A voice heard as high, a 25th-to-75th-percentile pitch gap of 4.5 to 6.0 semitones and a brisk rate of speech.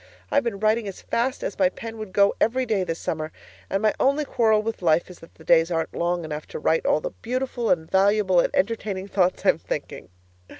Yes: high, 195 Hz; average, 4.8 semitones; fast, 220 wpm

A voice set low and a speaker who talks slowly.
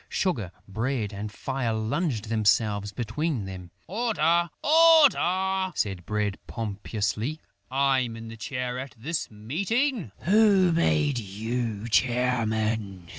Yes: low, 120 Hz; slow, 110 wpm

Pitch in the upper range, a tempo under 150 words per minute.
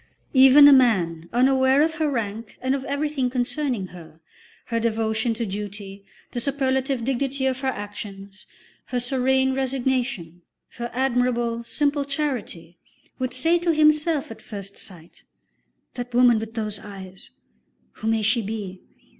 Yes: high, 245 Hz; average, 140 wpm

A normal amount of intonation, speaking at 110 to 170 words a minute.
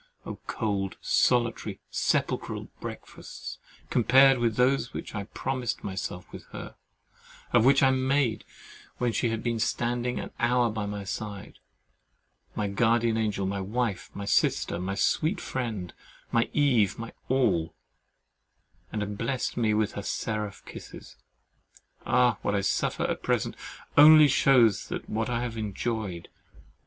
Yes: average, 3.3 semitones; average, 140 wpm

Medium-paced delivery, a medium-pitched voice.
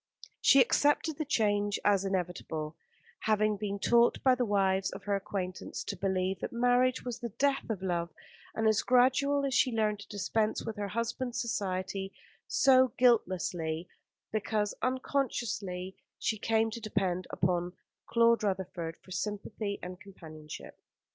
No: average, 145 wpm; high, 205 Hz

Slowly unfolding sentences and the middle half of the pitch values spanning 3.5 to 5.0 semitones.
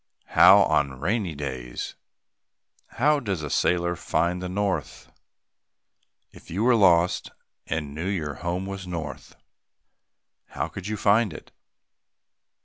Yes: slow, 125 wpm; average, 4.4 semitones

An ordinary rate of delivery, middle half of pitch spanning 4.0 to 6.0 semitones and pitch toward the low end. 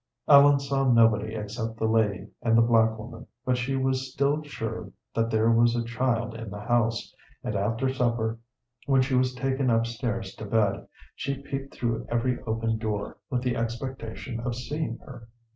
No: average, 175 wpm; narrow, 2.5 semitones; low, 115 Hz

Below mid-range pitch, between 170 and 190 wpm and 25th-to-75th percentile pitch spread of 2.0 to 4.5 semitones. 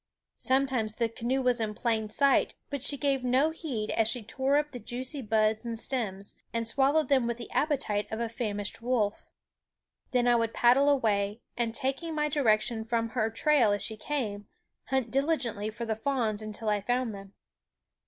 No: high, 235 Hz; average, 185 wpm; average, 3.6 semitones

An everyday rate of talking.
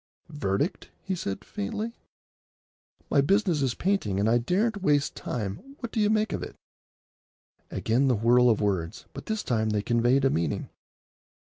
Yes: average, 160 wpm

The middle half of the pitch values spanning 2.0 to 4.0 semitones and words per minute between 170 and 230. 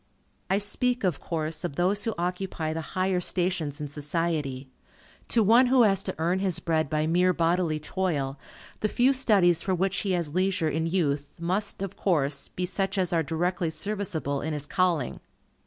Yes: average, 3.5 semitones; average, 180 wpm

